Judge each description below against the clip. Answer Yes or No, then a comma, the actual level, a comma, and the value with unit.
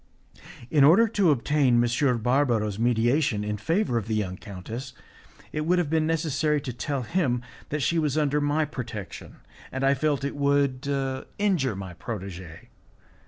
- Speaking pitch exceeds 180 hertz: No, low, 135 Hz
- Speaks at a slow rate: No, average, 160 wpm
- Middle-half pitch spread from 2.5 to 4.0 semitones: No, average, 4.8 semitones